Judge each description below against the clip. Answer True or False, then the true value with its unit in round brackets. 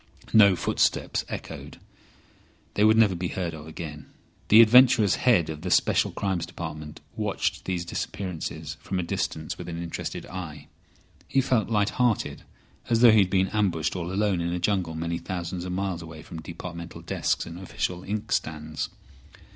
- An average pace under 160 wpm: False (165 wpm)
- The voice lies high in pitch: False (90 Hz)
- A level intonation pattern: False (3.3 semitones)